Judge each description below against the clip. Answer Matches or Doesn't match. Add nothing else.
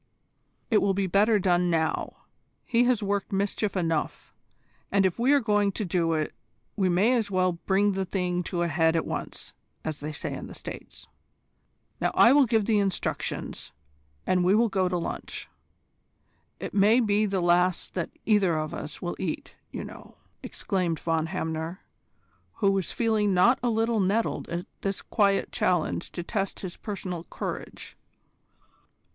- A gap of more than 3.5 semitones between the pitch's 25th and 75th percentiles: Doesn't match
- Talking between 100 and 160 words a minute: Doesn't match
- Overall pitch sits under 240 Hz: Matches